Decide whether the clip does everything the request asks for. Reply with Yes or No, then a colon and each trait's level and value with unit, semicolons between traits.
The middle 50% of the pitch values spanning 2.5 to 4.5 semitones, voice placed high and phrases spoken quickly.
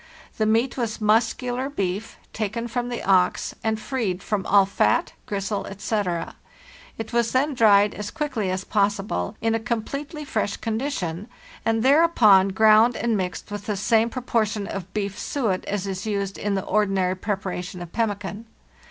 No: average, 2.9 semitones; high, 215 Hz; average, 160 wpm